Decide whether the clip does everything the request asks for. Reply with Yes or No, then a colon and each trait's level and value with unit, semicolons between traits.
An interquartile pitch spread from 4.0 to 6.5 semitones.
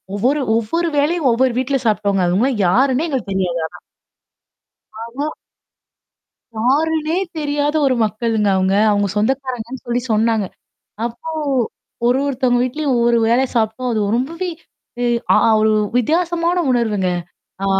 Yes: average, 4.7 semitones